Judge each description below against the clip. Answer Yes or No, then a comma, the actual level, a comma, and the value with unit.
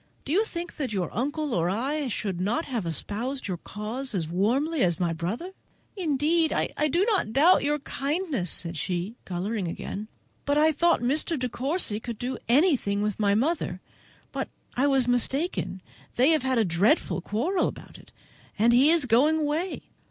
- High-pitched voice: Yes, very high, 255 Hz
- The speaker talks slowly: No, average, 175 wpm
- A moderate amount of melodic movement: No, wide, 6.9 semitones